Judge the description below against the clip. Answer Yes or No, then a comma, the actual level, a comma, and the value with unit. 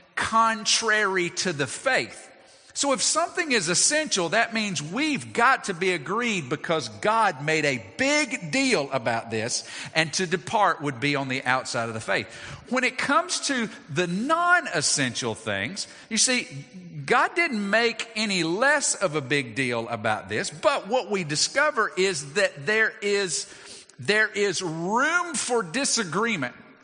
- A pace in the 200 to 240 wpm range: No, average, 155 wpm